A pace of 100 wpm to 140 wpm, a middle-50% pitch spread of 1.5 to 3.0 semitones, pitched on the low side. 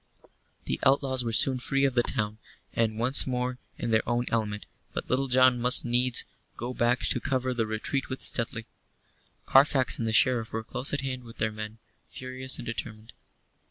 No: average, 185 wpm; narrow, 2.4 semitones; low, 125 Hz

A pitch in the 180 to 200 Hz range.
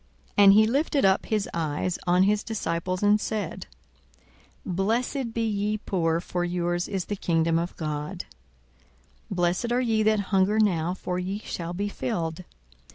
Yes: high, 190 Hz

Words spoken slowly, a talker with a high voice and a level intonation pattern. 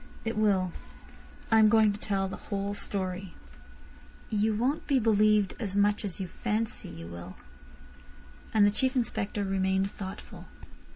No: average, 150 wpm; high, 205 Hz; narrow, 2.2 semitones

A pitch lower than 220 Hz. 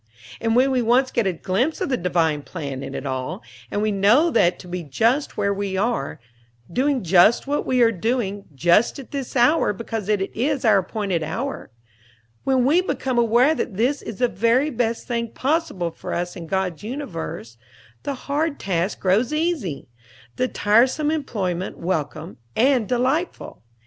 No: high, 230 Hz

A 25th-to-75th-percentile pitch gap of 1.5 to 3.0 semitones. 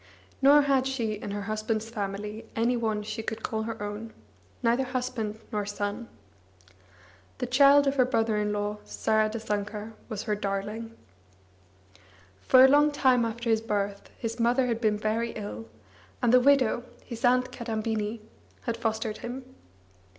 Yes: average, 2.7 semitones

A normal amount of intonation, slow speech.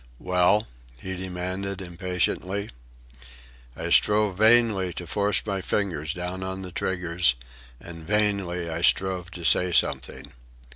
No: narrow, 2.1 semitones; slow, 125 wpm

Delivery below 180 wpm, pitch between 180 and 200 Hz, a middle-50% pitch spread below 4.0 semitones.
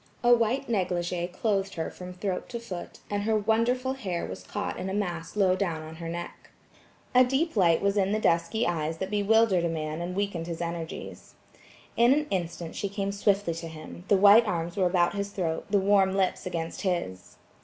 No: average, 195 wpm; high, 190 Hz; average, 3.4 semitones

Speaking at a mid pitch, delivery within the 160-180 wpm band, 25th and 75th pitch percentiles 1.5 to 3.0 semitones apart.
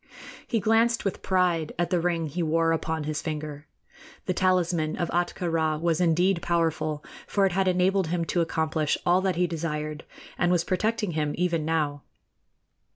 Yes: medium, 170 Hz; average, 170 wpm; narrow, 2.4 semitones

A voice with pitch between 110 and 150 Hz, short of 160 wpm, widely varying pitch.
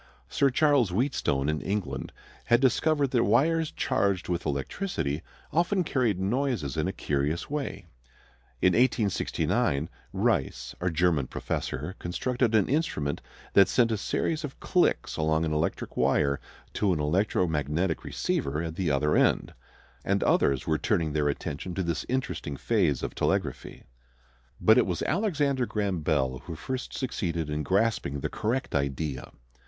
No: very low, 90 Hz; average, 145 wpm; wide, 8.9 semitones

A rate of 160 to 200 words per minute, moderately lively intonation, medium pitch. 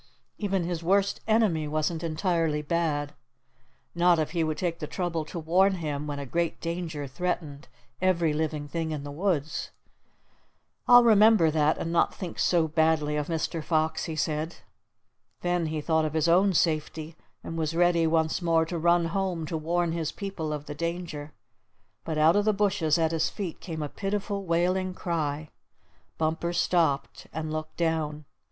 No: average, 170 wpm; narrow, 2.2 semitones; medium, 165 Hz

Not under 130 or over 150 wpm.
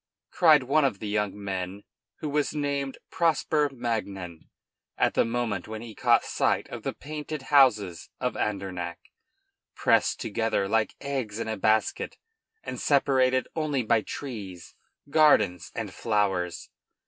Yes: average, 140 wpm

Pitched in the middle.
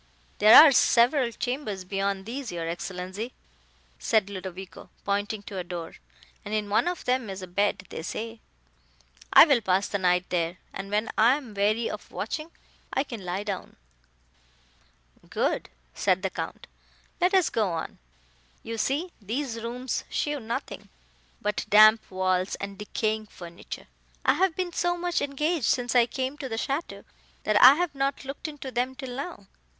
No: high, 220 Hz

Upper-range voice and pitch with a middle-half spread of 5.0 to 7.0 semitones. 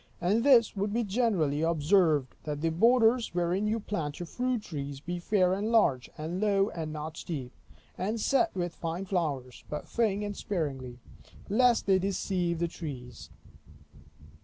No: medium, 180 Hz; wide, 5.4 semitones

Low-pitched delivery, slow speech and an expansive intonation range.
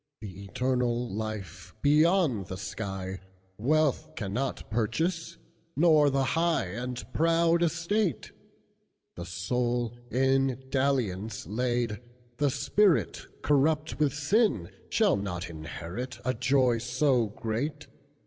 Yes: low, 125 Hz; slow, 90 wpm; wide, 6.0 semitones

